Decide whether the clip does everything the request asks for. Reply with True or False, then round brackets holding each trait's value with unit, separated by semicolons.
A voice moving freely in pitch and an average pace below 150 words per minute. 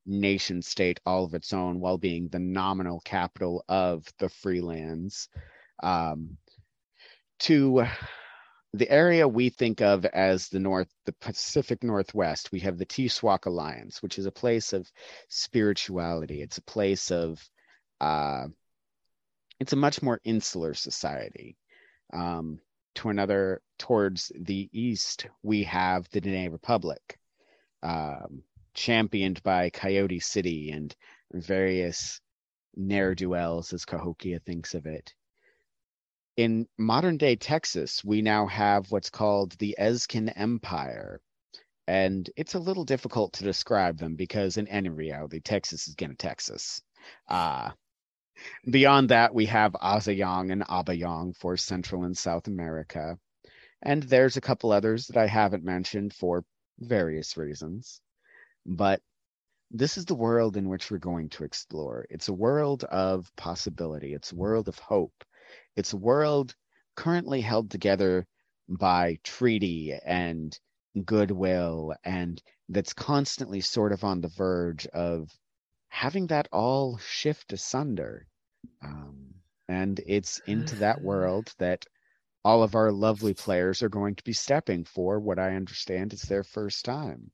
False (4.0 semitones; 135 wpm)